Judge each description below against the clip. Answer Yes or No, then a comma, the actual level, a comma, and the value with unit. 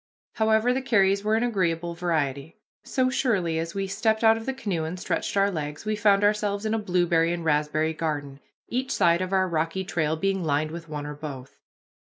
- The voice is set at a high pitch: No, medium, 180 Hz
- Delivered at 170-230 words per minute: Yes, fast, 205 wpm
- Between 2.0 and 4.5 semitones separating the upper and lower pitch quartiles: No, average, 5.0 semitones